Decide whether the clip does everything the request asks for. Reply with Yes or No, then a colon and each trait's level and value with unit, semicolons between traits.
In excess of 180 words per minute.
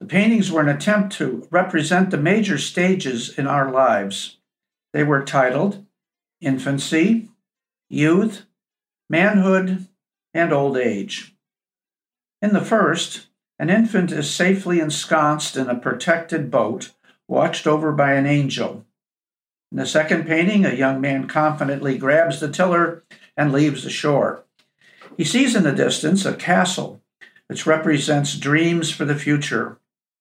No: slow, 135 wpm